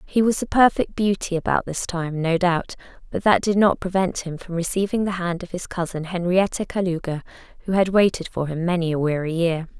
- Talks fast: Yes, fast, 210 wpm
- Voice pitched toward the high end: No, medium, 180 Hz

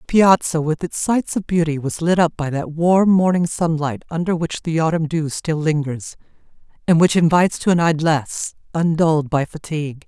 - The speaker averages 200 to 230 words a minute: No, average, 185 wpm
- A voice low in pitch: No, medium, 160 Hz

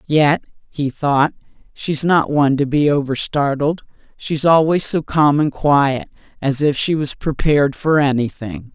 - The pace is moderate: Yes, average, 150 wpm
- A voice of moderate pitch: Yes, medium, 145 Hz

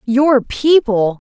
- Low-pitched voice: No, high, 245 Hz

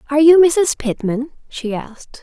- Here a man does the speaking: No, female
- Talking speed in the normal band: Yes, average, 160 wpm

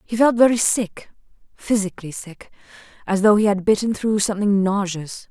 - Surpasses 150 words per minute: No, slow, 135 wpm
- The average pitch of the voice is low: No, high, 205 Hz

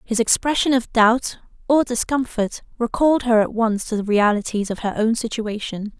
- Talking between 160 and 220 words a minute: No, average, 150 wpm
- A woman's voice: Yes, female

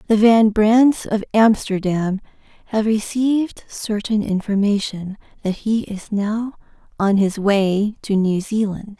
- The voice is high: Yes, high, 210 Hz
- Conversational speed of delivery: No, slow, 125 wpm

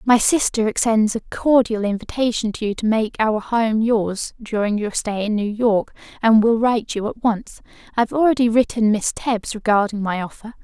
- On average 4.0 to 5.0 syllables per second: Yes, 4.9 syllables/s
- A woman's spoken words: Yes, female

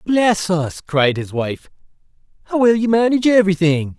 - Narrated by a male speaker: Yes, male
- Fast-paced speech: No, average, 150 wpm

